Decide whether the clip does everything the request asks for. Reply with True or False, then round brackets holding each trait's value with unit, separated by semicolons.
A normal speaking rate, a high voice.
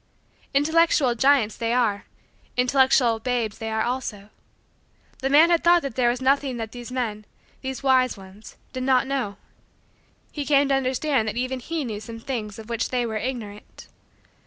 True (170 wpm; 250 Hz)